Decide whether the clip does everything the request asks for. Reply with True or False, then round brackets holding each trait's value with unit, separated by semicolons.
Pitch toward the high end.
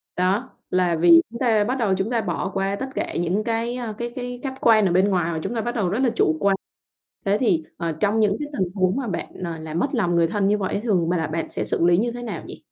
True (200 Hz)